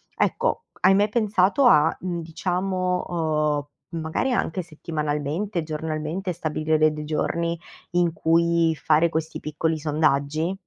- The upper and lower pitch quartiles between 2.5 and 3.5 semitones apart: Yes, average, 2.8 semitones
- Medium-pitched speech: Yes, medium, 165 Hz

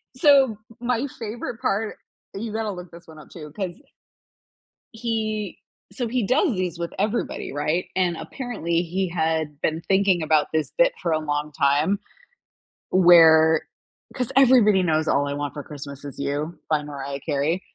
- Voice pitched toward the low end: No, medium, 170 Hz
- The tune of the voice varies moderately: No, wide, 6.0 semitones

